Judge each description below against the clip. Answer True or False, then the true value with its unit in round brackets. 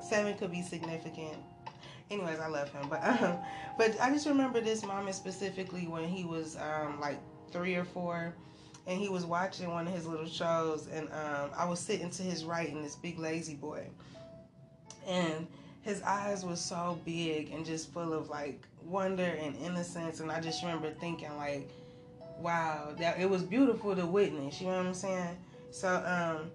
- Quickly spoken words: False (185 wpm)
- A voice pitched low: False (170 Hz)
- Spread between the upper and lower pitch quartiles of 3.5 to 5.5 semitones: False (2.7 semitones)